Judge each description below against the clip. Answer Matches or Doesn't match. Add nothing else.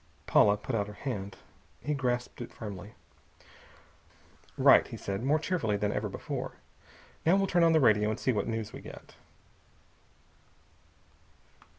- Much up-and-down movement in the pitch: Matches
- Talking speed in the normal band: Matches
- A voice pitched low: Matches